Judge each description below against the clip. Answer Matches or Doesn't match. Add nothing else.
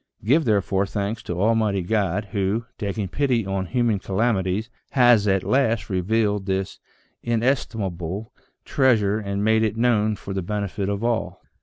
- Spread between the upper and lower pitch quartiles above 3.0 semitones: Doesn't match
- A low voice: Matches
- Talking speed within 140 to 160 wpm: Matches